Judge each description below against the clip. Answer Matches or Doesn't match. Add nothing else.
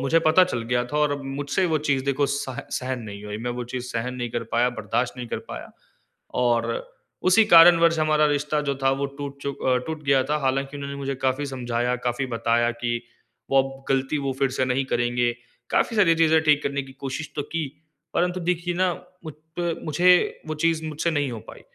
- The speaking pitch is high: Doesn't match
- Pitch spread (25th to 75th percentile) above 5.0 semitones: Doesn't match